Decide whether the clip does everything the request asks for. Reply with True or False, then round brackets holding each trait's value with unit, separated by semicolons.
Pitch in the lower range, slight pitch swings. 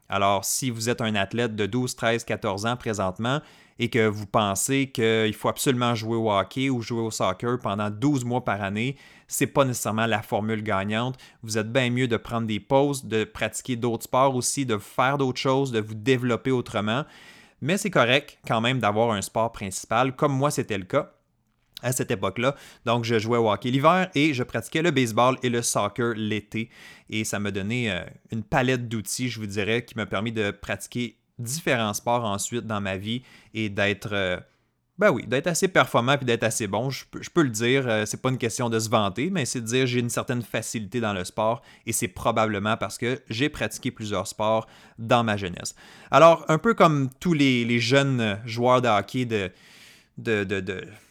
False (120 Hz; 3.1 semitones)